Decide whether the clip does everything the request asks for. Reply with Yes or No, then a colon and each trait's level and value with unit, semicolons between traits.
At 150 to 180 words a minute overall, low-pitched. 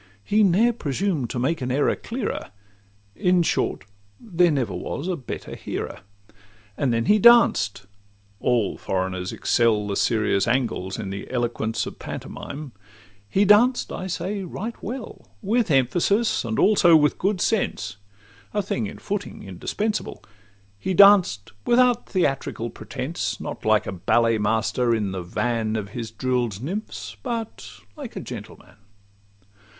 No: slow, 135 wpm; low, 125 Hz